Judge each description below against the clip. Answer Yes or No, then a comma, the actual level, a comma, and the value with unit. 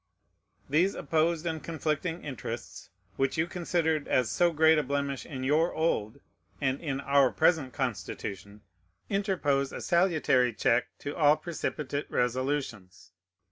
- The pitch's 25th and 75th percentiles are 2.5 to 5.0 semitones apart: Yes, average, 3.7 semitones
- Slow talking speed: Yes, slow, 130 wpm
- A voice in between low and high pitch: Yes, medium, 145 Hz